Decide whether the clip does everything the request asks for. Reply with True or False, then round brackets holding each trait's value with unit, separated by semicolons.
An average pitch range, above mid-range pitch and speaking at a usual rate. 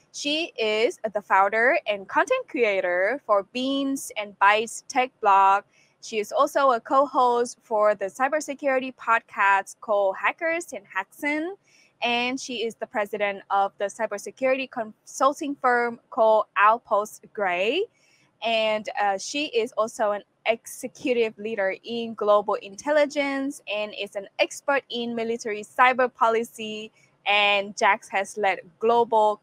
False (4.2 semitones; 220 Hz; 130 wpm)